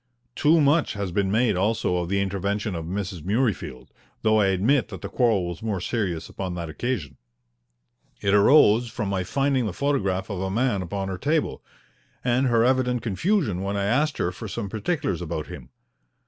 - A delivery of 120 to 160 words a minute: No, average, 185 wpm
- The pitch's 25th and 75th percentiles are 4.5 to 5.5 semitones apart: Yes, average, 4.9 semitones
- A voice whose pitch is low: Yes, low, 100 Hz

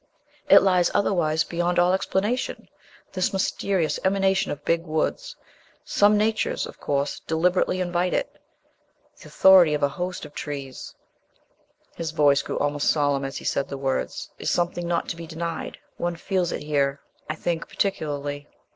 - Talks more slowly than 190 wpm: Yes, average, 155 wpm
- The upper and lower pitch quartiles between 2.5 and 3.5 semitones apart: No, average, 4.1 semitones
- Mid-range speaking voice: Yes, medium, 170 Hz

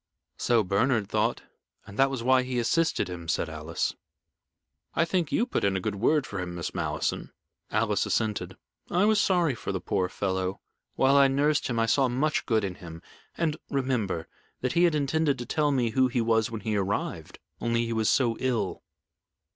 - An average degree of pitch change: No, wide, 5.7 semitones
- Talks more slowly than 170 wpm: No, average, 195 wpm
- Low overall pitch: Yes, low, 120 Hz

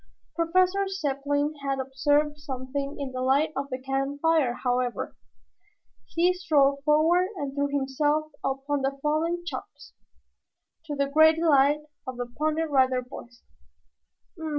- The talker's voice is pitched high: Yes, very high, 285 Hz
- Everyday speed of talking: No, slow, 130 wpm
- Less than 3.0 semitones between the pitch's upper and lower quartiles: Yes, narrow, 2.5 semitones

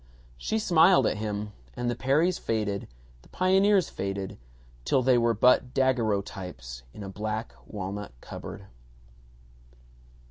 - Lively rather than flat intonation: No, average, 5.0 semitones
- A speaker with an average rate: No, slow, 120 wpm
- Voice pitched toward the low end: Yes, low, 110 Hz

